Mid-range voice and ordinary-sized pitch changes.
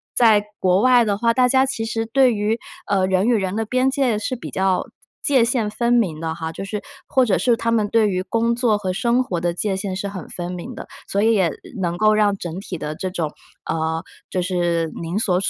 No: high, 205 Hz; average, 4.2 semitones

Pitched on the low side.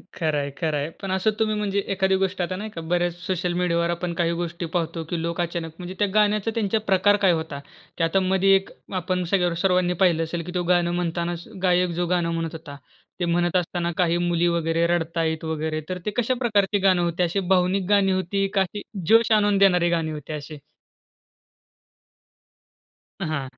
No: medium, 175 Hz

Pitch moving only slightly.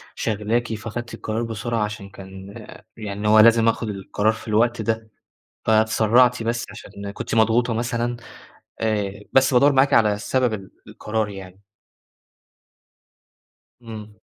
Yes: narrow, 1.9 semitones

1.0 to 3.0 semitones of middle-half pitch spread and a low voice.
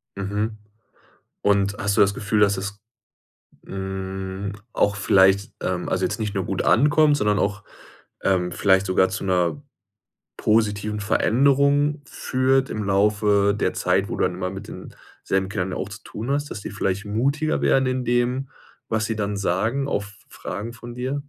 No: average, 3.9 semitones; low, 105 Hz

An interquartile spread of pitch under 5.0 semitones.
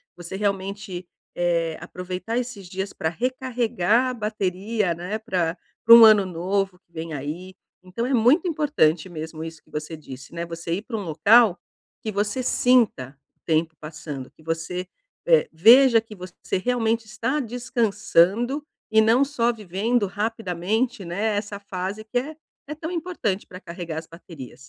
No: average, 5.3 semitones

